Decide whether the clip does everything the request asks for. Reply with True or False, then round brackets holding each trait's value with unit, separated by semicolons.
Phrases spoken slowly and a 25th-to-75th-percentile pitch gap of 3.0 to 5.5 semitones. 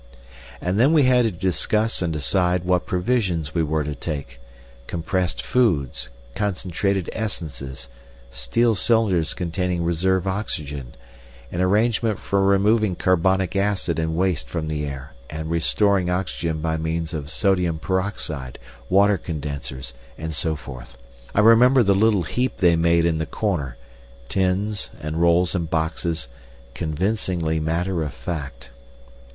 True (130 wpm; 4.2 semitones)